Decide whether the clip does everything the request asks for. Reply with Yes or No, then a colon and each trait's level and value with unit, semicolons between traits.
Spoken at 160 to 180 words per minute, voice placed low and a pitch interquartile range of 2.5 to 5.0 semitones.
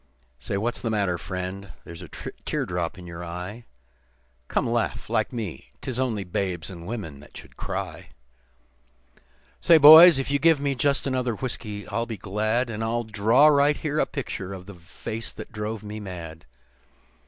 No: average, 175 wpm; low, 110 Hz; wide, 5.6 semitones